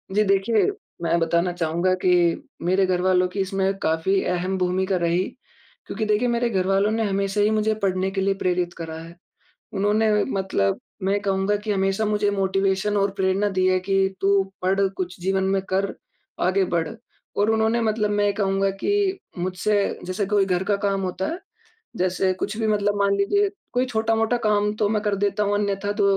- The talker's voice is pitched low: No, high, 195 Hz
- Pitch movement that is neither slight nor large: No, narrow, 1.9 semitones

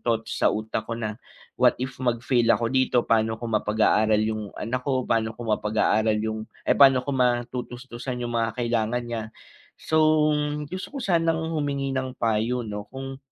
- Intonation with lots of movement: No, average, 2.8 semitones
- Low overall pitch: Yes, low, 120 Hz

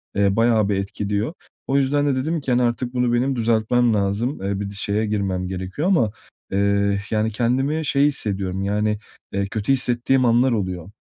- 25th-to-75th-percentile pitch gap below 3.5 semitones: No, average, 4.1 semitones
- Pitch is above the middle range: No, low, 110 Hz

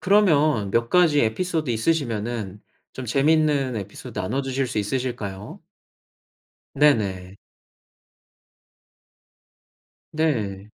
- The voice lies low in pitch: Yes, low, 125 Hz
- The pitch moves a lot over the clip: Yes, wide, 6.2 semitones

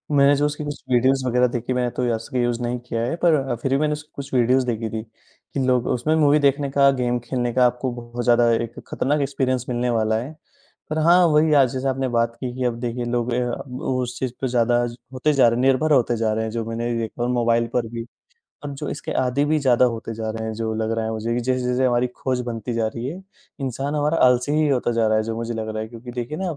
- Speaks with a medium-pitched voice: No, low, 125 Hz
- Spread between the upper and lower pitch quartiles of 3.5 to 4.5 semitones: No, narrow, 2.4 semitones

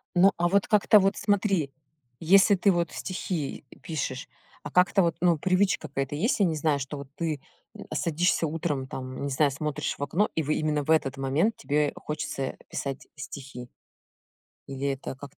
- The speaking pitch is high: No, medium, 155 Hz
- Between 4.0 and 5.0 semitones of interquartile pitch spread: Yes, average, 4.6 semitones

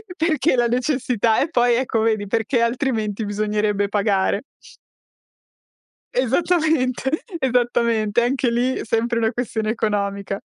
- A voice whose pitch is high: Yes, high, 235 Hz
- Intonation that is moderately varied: Yes, average, 3.2 semitones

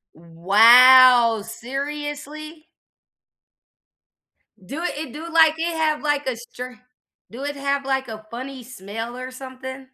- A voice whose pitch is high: Yes, very high, 260 Hz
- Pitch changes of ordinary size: Yes, average, 3.6 semitones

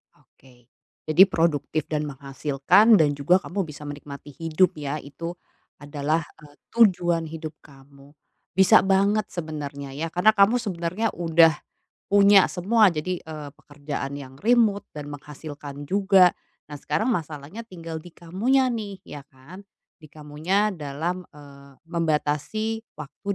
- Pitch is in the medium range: Yes, medium, 160 Hz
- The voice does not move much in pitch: No, average, 4.8 semitones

